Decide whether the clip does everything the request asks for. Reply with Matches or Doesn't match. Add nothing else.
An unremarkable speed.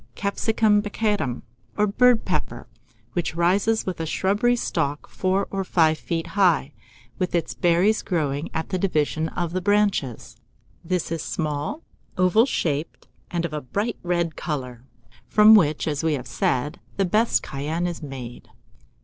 Matches